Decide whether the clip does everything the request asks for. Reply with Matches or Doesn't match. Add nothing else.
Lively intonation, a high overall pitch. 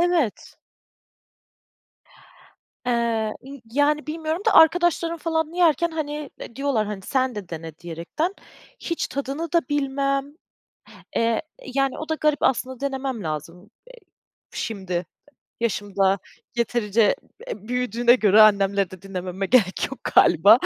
Matches